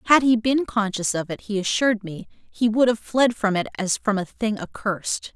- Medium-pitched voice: No, high, 215 Hz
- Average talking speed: No, fast, 225 wpm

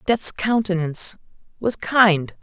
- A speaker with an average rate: No, slow, 100 wpm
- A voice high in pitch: Yes, high, 195 Hz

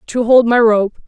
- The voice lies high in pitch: Yes, high, 230 Hz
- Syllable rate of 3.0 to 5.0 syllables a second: Yes, 4.4 syllables/s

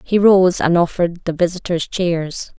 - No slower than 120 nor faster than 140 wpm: No, average, 160 wpm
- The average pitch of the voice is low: No, medium, 175 Hz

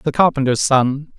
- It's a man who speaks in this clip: Yes, male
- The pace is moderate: Yes, average, 150 wpm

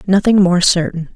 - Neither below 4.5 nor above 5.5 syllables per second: Yes, 5.1 syllables/s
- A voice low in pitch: No, medium, 180 Hz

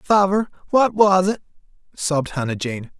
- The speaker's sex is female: No, male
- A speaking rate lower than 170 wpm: Yes, average, 140 wpm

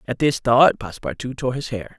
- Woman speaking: No, male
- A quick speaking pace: Yes, fast, 210 wpm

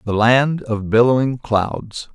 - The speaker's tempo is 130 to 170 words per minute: Yes, average, 140 wpm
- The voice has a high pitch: No, low, 120 Hz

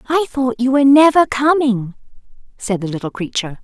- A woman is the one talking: Yes, female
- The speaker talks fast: No, average, 165 wpm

